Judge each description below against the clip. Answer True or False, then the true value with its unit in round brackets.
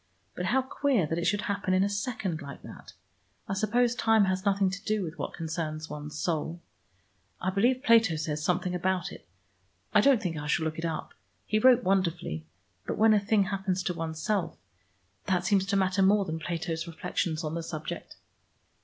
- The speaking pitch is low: False (185 Hz)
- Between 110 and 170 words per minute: False (190 wpm)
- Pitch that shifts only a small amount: False (3.8 semitones)